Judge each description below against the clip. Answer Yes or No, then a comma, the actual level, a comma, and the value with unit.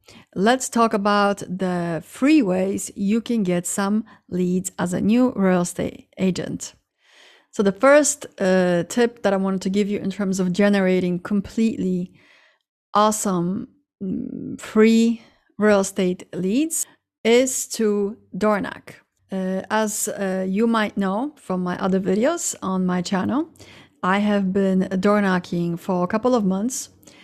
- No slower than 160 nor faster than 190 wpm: No, average, 145 wpm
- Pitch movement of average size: Yes, average, 3.3 semitones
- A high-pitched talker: Yes, high, 200 Hz